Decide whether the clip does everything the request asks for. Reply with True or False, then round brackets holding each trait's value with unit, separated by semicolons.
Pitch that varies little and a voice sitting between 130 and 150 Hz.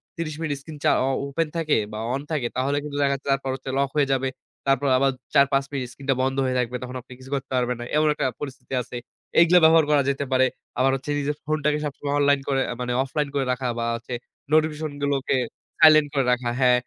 True (2.3 semitones; 140 Hz)